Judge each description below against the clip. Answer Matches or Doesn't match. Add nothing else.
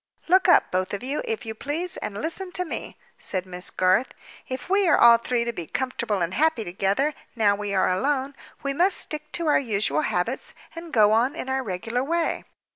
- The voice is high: Matches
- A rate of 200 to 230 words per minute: Matches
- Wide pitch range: Matches